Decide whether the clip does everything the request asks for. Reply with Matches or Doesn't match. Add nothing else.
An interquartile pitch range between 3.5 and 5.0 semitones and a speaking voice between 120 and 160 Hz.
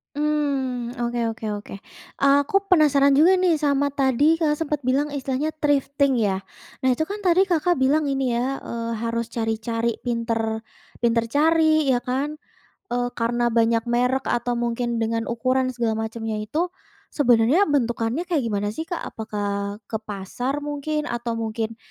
Doesn't match